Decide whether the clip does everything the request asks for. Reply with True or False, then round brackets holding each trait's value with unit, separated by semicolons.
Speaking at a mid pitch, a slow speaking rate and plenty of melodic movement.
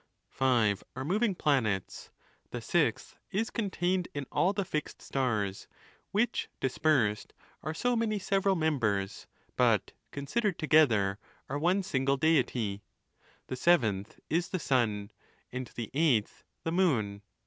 True (145 Hz; 130 wpm; 8.3 semitones)